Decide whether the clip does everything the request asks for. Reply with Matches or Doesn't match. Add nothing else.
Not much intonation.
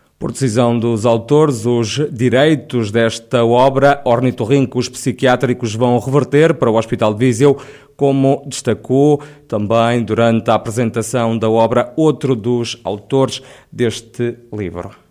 Doesn't match